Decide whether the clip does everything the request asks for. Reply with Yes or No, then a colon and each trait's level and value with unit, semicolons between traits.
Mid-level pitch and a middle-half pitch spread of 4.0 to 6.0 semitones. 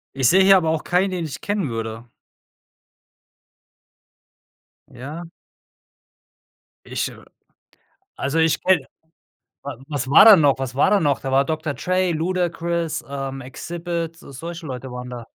Yes: medium, 160 Hz; average, 4.4 semitones